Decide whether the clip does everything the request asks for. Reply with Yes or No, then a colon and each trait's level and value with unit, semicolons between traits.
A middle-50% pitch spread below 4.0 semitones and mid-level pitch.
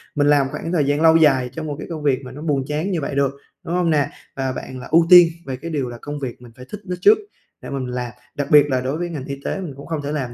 Yes: average, 3.5 semitones; medium, 145 Hz